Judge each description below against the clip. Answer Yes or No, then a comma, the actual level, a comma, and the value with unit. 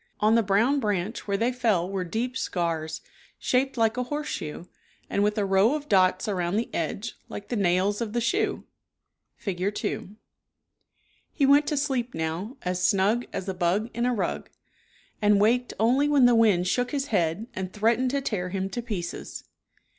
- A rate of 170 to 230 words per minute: Yes, average, 185 wpm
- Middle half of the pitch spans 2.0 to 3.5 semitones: No, average, 4.8 semitones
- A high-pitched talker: Yes, high, 210 Hz